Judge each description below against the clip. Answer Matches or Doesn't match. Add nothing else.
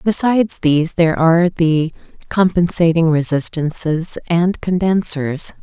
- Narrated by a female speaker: Matches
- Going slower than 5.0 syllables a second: Matches